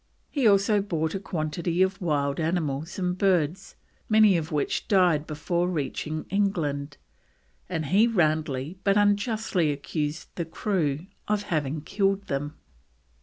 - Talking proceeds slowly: Yes, slow, 130 wpm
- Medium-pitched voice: Yes, medium, 170 Hz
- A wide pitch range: No, average, 4.5 semitones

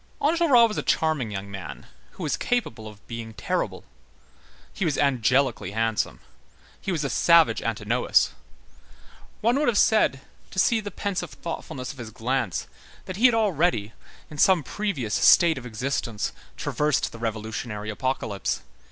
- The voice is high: No, low, 135 Hz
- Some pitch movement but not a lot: No, wide, 9.0 semitones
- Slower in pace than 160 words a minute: Yes, average, 150 wpm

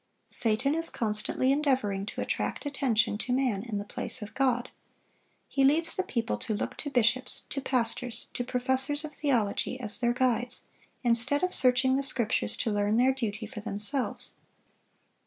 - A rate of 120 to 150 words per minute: No, average, 165 wpm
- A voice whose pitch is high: Yes, very high, 250 Hz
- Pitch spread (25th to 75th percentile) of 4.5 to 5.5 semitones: No, average, 3.4 semitones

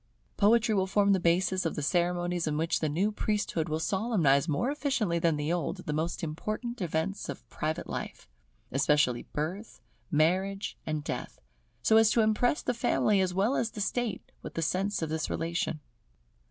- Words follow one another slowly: No, average, 180 wpm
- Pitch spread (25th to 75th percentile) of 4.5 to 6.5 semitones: Yes, average, 4.9 semitones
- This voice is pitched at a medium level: Yes, medium, 180 Hz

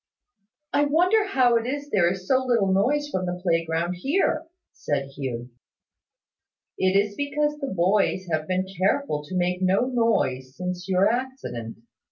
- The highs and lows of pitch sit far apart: Yes, wide, 7.2 semitones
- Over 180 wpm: No, average, 155 wpm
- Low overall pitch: No, high, 190 Hz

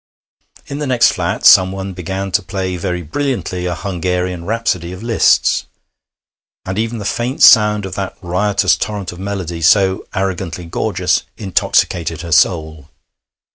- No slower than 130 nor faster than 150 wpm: Yes, average, 140 wpm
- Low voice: Yes, very low, 95 Hz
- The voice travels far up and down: No, average, 2.8 semitones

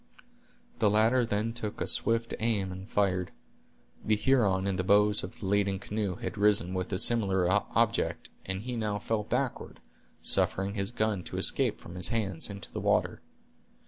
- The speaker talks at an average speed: Yes, average, 175 wpm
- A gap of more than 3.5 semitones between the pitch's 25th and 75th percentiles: No, narrow, 2.5 semitones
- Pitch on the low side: Yes, low, 105 Hz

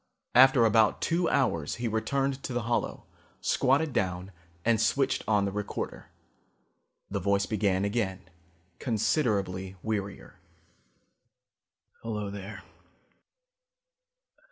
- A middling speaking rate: No, slow, 100 wpm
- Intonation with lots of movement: No, average, 3.8 semitones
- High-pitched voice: No, low, 110 Hz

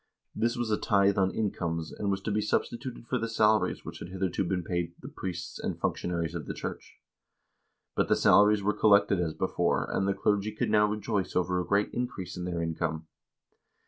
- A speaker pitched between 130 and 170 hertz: No, very low, 95 Hz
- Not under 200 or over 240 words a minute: Yes, fast, 205 wpm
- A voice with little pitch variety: No, average, 3.3 semitones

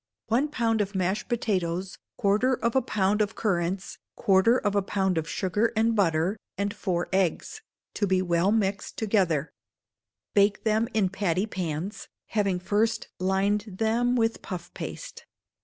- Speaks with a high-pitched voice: Yes, high, 200 Hz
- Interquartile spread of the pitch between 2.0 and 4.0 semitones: Yes, average, 3.0 semitones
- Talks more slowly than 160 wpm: Yes, average, 150 wpm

